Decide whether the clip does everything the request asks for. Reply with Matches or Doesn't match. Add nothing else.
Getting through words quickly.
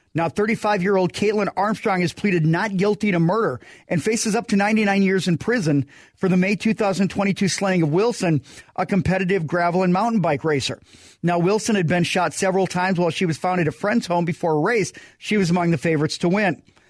Matches